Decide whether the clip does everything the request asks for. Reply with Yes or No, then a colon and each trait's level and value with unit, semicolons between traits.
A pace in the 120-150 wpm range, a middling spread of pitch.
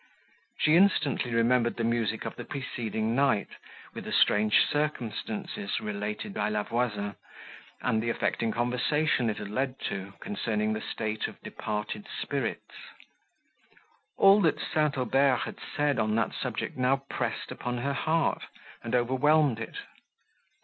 Yes: average, 140 wpm; average, 4.6 semitones